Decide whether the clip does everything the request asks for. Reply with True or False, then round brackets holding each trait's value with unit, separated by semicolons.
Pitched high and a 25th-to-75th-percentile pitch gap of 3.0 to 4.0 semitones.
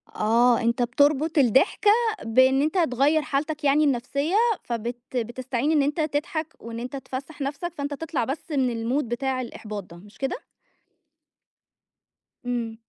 True (265 Hz; 3.6 semitones)